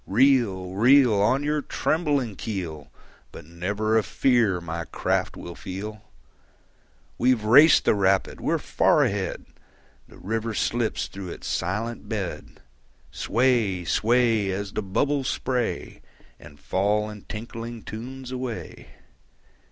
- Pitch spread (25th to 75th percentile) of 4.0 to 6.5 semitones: Yes, average, 4.3 semitones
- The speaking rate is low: Yes, slow, 120 wpm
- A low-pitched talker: Yes, low, 110 Hz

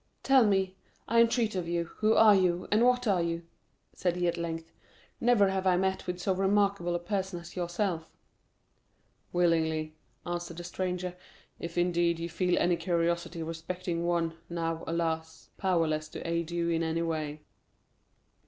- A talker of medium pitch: Yes, medium, 175 Hz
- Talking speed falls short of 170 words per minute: Yes, average, 155 wpm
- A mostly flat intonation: Yes, narrow, 2.2 semitones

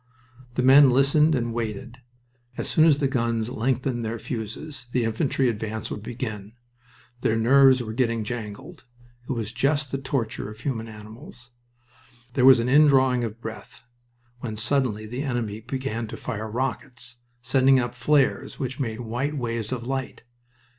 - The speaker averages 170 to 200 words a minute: No, average, 155 wpm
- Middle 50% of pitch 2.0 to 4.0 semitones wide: Yes, average, 3.0 semitones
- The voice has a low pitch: Yes, low, 120 Hz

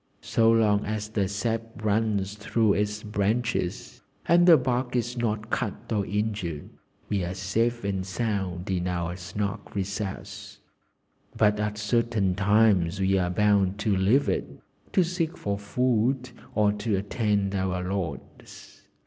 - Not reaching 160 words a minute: Yes, average, 140 wpm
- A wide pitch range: No, average, 2.7 semitones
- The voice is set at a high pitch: No, low, 105 Hz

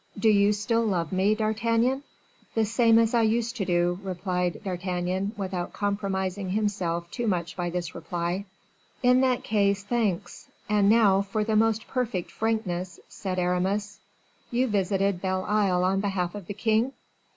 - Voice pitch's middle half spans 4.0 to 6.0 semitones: No, average, 3.3 semitones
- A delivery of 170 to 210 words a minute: No, average, 155 wpm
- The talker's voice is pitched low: No, high, 200 Hz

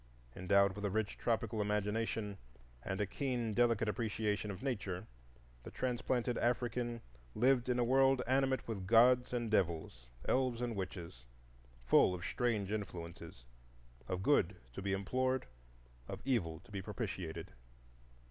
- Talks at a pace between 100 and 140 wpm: Yes, slow, 135 wpm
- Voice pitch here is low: Yes, low, 105 Hz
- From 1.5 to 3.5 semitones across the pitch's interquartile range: No, average, 4.5 semitones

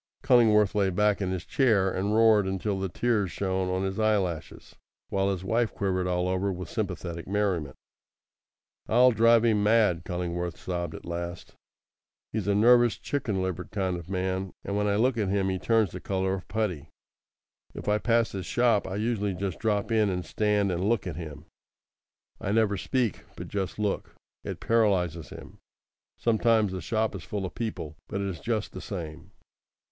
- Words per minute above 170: Yes, average, 180 wpm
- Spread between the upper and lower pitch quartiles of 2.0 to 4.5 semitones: Yes, average, 3.0 semitones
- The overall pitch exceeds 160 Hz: No, low, 100 Hz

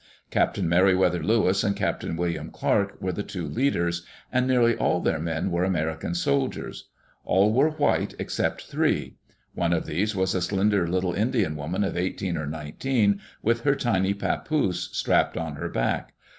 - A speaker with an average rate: Yes, average, 170 wpm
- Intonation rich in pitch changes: No, average, 4.3 semitones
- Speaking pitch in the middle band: No, very low, 95 Hz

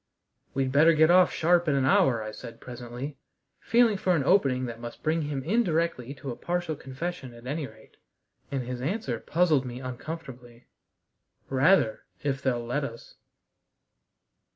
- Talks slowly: No, average, 155 wpm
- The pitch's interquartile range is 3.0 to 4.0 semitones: No, average, 4.8 semitones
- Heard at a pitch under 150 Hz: Yes, low, 135 Hz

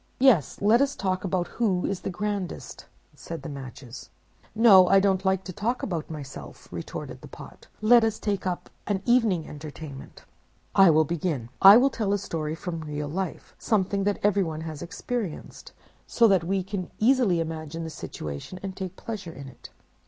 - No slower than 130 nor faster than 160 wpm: No, average, 175 wpm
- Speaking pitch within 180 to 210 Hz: Yes, medium, 185 Hz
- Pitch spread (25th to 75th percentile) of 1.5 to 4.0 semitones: No, average, 4.4 semitones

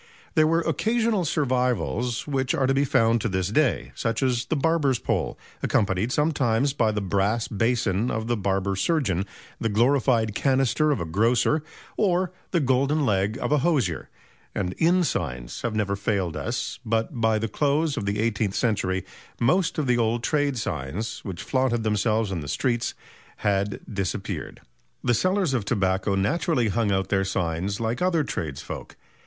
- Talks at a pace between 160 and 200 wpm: Yes, average, 165 wpm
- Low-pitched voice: Yes, low, 115 Hz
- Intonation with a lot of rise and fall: Yes, wide, 5.8 semitones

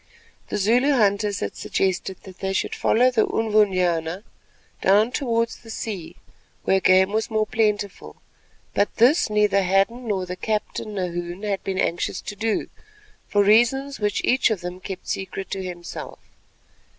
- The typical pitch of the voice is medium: No, high, 205 Hz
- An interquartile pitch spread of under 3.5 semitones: Yes, average, 2.8 semitones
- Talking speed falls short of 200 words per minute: Yes, average, 150 wpm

